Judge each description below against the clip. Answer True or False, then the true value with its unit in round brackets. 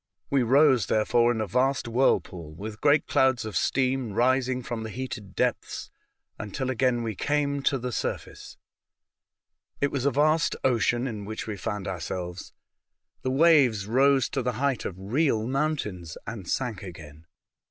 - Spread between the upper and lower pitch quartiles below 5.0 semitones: True (4.2 semitones)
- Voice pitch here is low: True (120 Hz)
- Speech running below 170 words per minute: True (160 wpm)